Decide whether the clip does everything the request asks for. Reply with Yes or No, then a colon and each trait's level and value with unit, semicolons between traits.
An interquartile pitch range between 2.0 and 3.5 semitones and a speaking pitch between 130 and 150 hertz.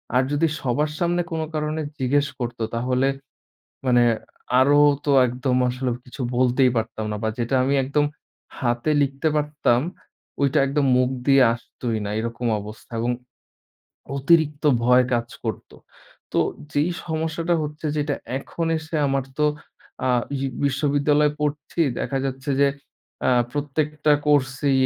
Yes: average, 3.1 semitones; medium, 140 Hz